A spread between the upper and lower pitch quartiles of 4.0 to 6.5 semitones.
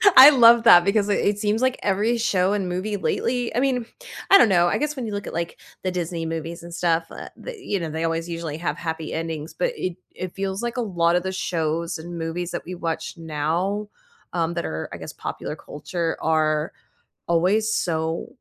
Yes: average, 4.3 semitones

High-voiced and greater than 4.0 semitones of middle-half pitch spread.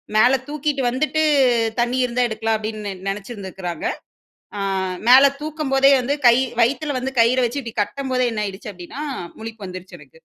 Yes: high, 240 Hz; average, 4.4 semitones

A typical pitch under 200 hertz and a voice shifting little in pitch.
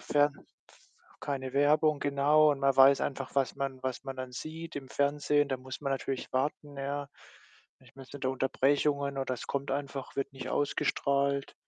Yes: medium, 140 Hz; narrow, 1.4 semitones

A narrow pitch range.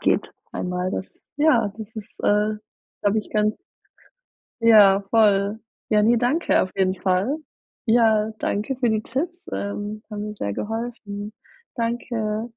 Yes: narrow, 2.2 semitones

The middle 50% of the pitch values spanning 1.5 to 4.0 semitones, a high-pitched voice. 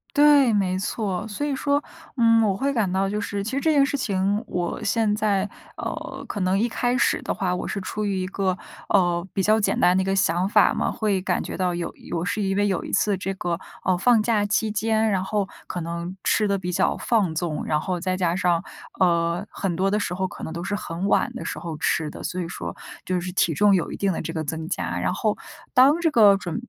Yes: average, 3.2 semitones; high, 195 Hz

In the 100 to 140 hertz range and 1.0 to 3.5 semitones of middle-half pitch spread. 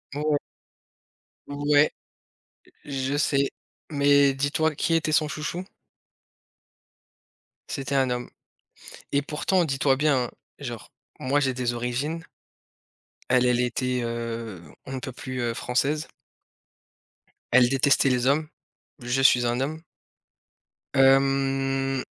Yes: low, 135 Hz; narrow, 2.4 semitones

